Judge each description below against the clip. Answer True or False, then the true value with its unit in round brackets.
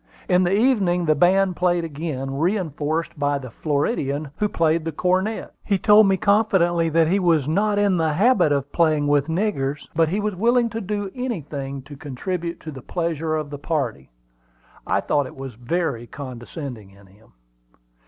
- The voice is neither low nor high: True (165 Hz)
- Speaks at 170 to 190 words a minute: True (175 wpm)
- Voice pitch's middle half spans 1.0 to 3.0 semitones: False (5.0 semitones)